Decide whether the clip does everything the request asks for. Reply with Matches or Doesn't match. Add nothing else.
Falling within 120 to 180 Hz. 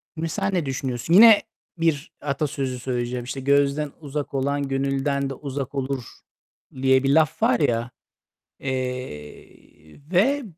Matches